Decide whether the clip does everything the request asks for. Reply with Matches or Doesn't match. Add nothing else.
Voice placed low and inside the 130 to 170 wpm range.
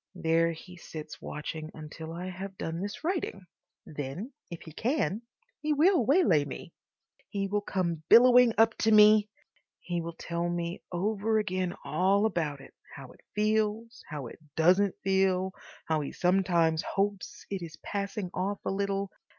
Doesn't match